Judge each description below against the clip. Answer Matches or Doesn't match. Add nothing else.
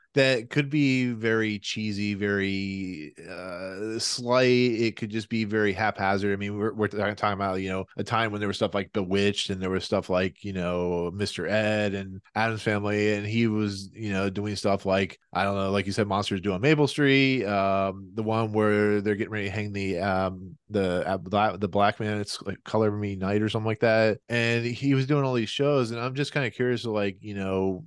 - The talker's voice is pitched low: Matches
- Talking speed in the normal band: Doesn't match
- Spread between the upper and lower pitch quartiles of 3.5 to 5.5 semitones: Doesn't match